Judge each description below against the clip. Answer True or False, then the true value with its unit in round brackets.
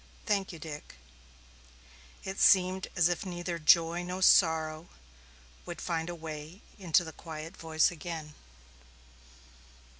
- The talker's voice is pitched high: False (170 Hz)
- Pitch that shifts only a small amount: True (2.1 semitones)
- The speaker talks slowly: True (120 wpm)